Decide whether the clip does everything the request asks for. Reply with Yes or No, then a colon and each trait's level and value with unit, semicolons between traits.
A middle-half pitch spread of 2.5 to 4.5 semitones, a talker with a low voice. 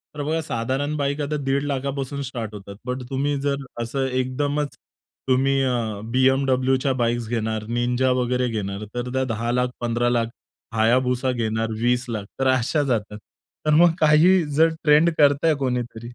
Yes: average, 3.1 semitones; low, 130 Hz